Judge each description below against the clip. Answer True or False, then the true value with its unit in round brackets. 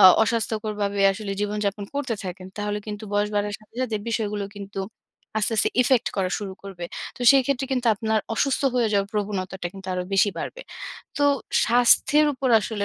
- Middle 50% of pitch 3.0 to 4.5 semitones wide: False (2.6 semitones)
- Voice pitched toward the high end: True (210 Hz)